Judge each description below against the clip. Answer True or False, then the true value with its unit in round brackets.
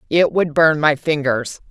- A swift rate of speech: False (175 wpm)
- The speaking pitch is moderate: True (150 Hz)